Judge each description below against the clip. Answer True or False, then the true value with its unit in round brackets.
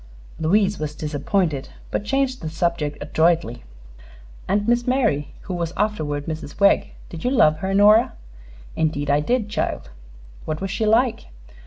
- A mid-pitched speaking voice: True (175 Hz)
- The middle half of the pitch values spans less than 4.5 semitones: False (5.6 semitones)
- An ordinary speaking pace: True (150 wpm)